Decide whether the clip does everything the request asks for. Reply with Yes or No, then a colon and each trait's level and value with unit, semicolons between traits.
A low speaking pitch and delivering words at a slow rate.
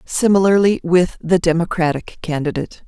No: medium, 175 Hz; slow, 105 wpm